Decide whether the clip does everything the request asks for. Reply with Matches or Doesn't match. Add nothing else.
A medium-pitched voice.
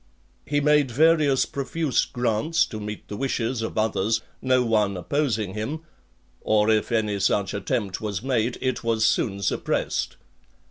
Doesn't match